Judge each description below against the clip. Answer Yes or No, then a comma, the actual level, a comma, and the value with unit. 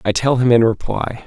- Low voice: Yes, low, 120 Hz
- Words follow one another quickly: Yes, fast, 235 wpm